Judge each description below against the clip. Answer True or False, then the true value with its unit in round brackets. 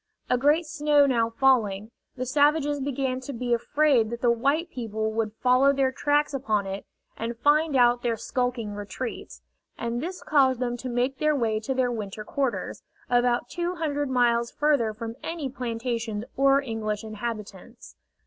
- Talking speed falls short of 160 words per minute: False (165 wpm)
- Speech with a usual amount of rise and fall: True (3.6 semitones)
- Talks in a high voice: True (250 Hz)